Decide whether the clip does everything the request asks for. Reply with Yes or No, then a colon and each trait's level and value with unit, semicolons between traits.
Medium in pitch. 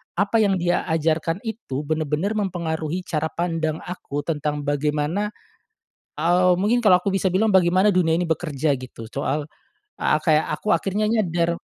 Yes: medium, 170 Hz